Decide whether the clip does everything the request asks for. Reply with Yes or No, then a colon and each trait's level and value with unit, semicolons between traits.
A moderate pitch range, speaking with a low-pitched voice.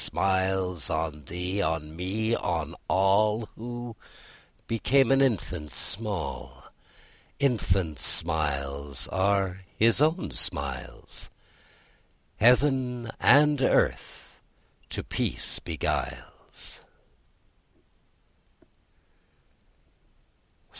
No: wide, 6.7 semitones; very low, 95 Hz